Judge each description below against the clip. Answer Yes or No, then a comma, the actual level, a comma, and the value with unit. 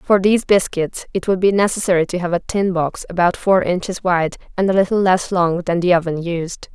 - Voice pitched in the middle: Yes, medium, 180 Hz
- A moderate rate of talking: No, fast, 220 wpm